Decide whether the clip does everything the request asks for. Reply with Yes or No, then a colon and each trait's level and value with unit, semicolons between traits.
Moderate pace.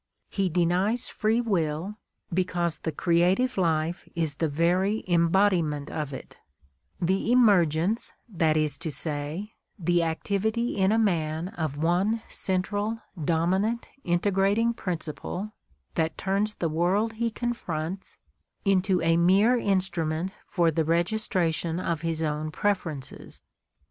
No: slow, 125 wpm